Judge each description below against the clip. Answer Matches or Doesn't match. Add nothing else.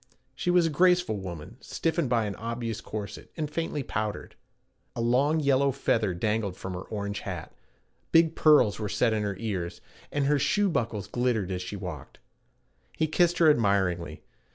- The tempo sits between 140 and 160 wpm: Doesn't match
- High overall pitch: Doesn't match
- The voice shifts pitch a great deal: Matches